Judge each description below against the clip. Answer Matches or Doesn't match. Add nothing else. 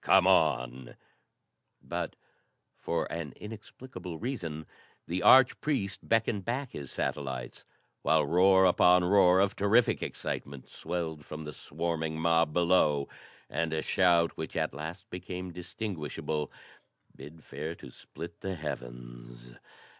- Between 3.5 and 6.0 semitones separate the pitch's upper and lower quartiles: Matches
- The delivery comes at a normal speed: Doesn't match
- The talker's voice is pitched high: Doesn't match